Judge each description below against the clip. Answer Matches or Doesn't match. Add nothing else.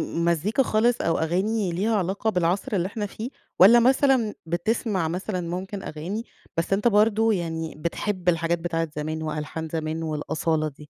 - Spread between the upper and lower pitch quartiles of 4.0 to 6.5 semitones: Matches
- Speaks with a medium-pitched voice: Matches